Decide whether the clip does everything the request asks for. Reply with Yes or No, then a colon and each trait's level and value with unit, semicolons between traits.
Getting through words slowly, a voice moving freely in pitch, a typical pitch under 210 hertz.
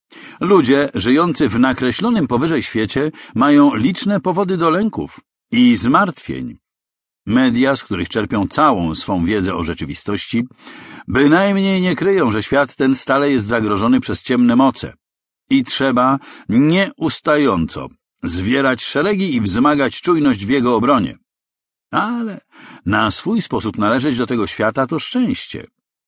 Yes: slow, 125 wpm; wide, 8.6 semitones; medium, 140 Hz